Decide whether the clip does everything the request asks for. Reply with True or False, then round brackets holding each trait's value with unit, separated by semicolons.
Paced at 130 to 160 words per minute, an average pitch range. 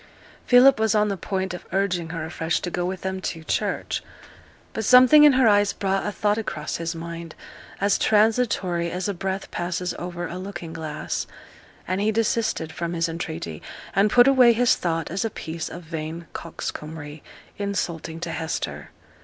False (175 wpm; 3.9 semitones)